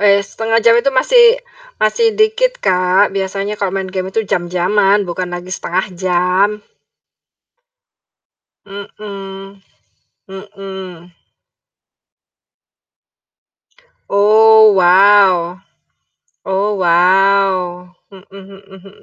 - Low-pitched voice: No, high, 195 Hz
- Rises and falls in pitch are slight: Yes, narrow, 2.0 semitones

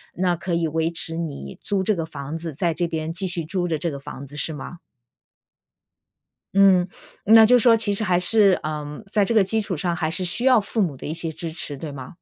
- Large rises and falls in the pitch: No, average, 3.8 semitones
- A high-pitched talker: No, medium, 170 Hz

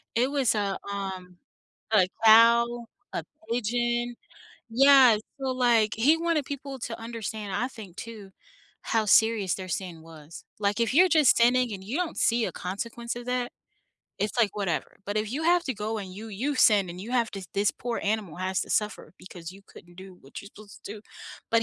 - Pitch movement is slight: No, average, 3.6 semitones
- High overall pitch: Yes, high, 220 Hz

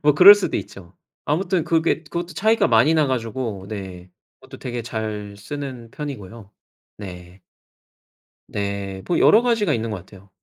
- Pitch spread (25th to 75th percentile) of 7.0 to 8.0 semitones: Yes, wide, 7.7 semitones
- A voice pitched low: Yes, low, 115 Hz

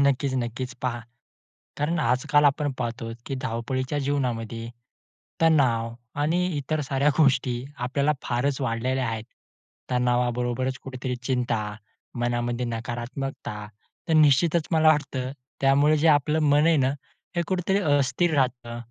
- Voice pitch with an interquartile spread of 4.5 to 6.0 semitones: No, average, 3.2 semitones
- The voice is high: No, low, 130 Hz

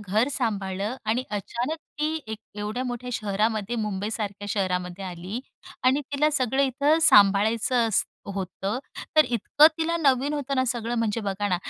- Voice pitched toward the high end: Yes, high, 225 Hz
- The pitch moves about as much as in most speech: Yes, average, 4.3 semitones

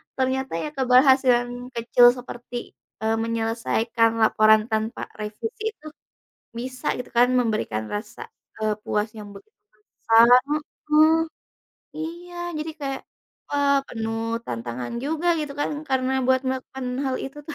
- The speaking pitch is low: No, high, 245 Hz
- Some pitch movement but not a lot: Yes, average, 3.6 semitones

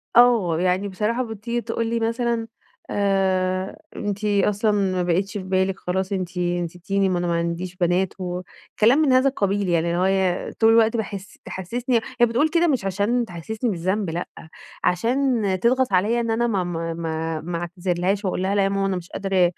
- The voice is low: No, high, 195 Hz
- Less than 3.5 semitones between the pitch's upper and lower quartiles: No, average, 4.1 semitones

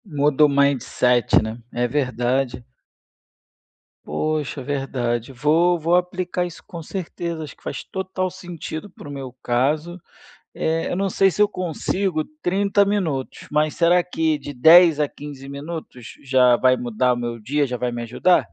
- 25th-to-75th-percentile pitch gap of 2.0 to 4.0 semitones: No, wide, 5.4 semitones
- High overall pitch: No, medium, 150 Hz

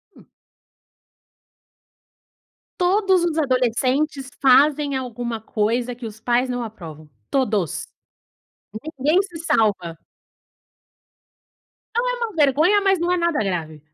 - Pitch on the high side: Yes, very high, 260 Hz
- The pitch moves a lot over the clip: Yes, wide, 6.8 semitones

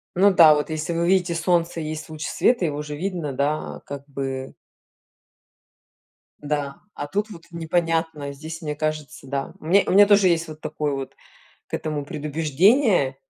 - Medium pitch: Yes, medium, 155 Hz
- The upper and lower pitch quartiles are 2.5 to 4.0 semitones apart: Yes, average, 2.8 semitones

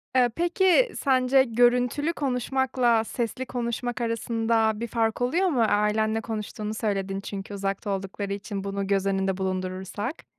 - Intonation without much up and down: No, average, 3.9 semitones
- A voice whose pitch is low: No, high, 225 Hz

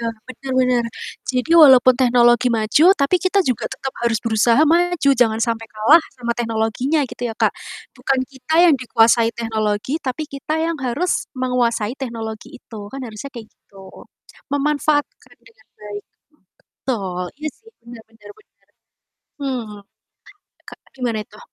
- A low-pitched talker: No, high, 240 Hz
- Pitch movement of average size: Yes, average, 3.3 semitones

